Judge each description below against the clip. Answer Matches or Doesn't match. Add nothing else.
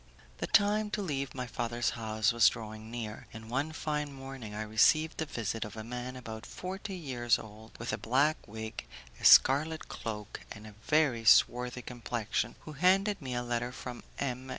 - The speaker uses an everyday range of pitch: Matches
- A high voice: Doesn't match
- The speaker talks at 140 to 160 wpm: Doesn't match